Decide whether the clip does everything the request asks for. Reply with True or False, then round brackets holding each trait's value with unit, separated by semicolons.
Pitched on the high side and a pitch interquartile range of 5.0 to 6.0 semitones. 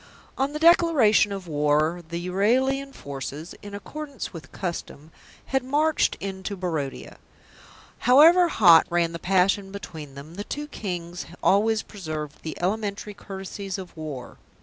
True (195 Hz; 5.3 semitones)